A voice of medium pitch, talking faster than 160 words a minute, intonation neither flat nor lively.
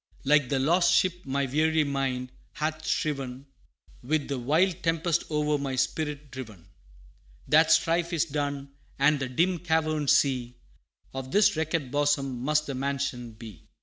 No: medium, 145 Hz; average, 150 wpm; average, 3.0 semitones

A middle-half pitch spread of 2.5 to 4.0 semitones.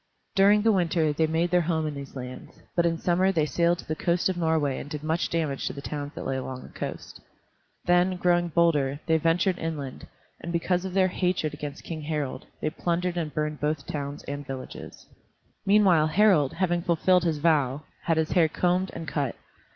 Yes: average, 3.1 semitones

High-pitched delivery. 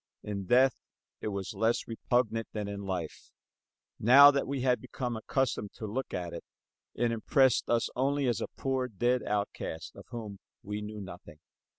No: low, 115 Hz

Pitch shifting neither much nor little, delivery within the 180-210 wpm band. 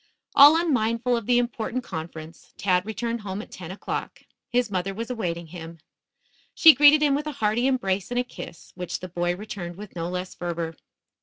No: wide, 5.7 semitones; average, 185 wpm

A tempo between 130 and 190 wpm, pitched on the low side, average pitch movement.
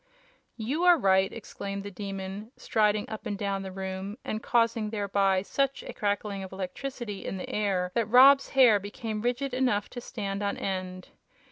No: average, 170 wpm; high, 205 Hz; average, 3.1 semitones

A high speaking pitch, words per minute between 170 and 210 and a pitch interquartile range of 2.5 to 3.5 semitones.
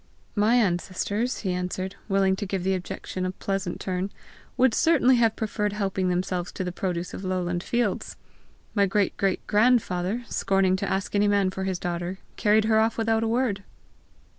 Yes: high, 195 Hz; average, 175 wpm; average, 2.9 semitones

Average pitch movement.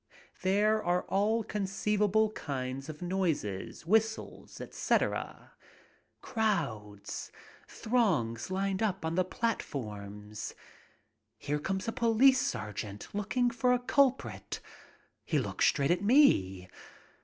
No: wide, 8.9 semitones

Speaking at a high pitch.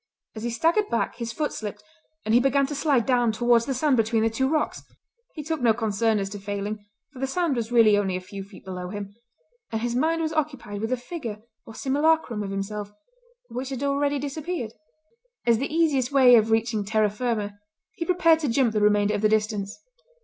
Yes: high, 235 Hz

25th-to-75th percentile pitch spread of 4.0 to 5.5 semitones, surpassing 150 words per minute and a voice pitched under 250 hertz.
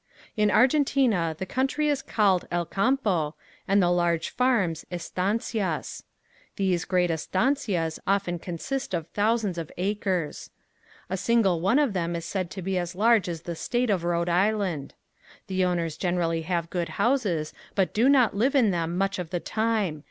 Yes: average, 4.3 semitones; average, 160 wpm; medium, 185 Hz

